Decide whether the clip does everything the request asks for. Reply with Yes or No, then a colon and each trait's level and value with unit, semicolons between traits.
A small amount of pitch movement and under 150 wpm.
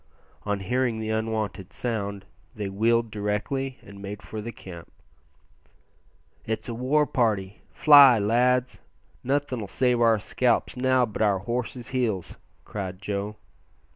No: average, 3.5 semitones; slow, 135 wpm